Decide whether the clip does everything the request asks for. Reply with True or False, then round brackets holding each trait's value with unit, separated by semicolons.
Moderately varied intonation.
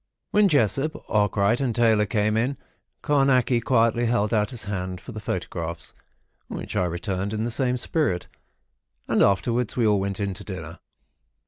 True (3.8 semitones)